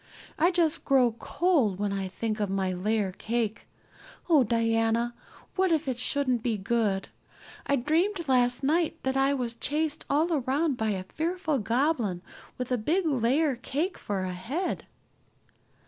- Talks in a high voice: Yes, very high, 250 Hz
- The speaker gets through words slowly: No, average, 155 wpm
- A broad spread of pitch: Yes, wide, 5.9 semitones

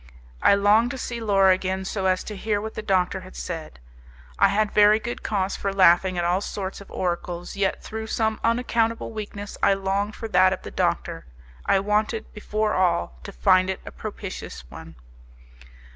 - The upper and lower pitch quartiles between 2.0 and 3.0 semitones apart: Yes, narrow, 2.5 semitones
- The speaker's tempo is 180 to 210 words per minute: Yes, average, 185 wpm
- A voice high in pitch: Yes, high, 200 Hz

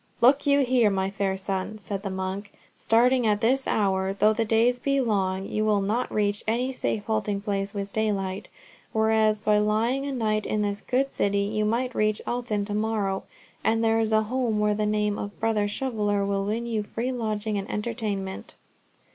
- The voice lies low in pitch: No, high, 215 Hz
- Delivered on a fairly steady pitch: Yes, narrow, 2.2 semitones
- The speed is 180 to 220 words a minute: Yes, average, 190 wpm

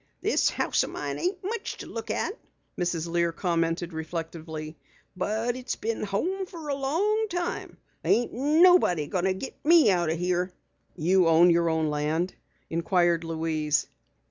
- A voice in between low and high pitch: Yes, medium, 180 Hz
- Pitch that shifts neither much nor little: No, wide, 8.6 semitones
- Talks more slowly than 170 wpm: Yes, average, 155 wpm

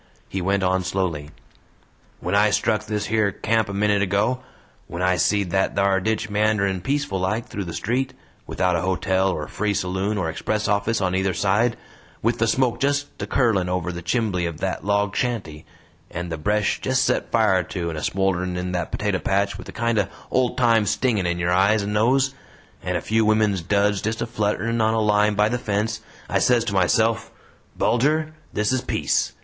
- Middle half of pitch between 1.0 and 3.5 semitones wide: Yes, average, 3.1 semitones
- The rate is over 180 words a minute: Yes, average, 200 wpm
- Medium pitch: No, low, 105 Hz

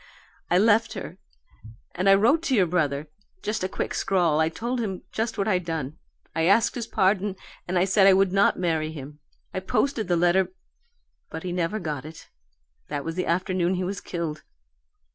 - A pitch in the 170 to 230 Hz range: Yes, medium, 185 Hz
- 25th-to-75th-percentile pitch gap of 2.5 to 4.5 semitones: Yes, average, 3.5 semitones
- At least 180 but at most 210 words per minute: Yes, average, 190 wpm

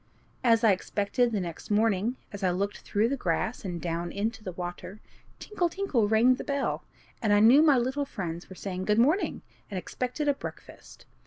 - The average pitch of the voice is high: Yes, high, 215 Hz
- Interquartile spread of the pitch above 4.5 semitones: Yes, average, 5.1 semitones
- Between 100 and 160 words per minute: No, average, 190 wpm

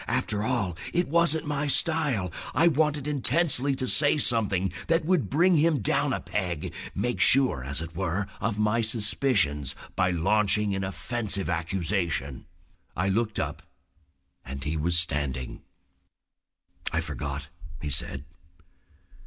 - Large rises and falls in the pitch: Yes, wide, 8.8 semitones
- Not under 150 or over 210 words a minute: No, slow, 135 wpm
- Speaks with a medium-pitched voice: No, low, 105 Hz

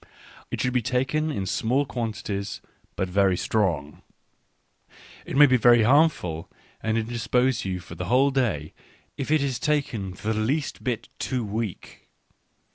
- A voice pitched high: No, low, 115 Hz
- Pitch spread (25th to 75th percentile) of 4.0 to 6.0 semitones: Yes, average, 5.0 semitones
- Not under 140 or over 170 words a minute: Yes, average, 150 wpm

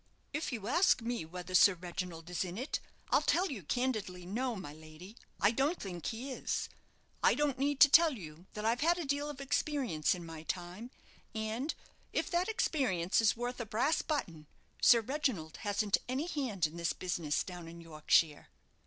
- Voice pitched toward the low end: No, high, 215 Hz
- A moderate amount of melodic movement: No, wide, 7.8 semitones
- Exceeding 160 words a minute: Yes, average, 185 wpm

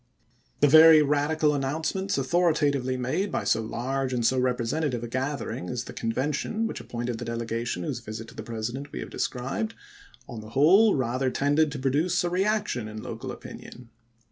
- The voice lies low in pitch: Yes, low, 130 Hz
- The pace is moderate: Yes, average, 170 wpm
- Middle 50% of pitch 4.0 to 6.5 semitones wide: Yes, average, 4.6 semitones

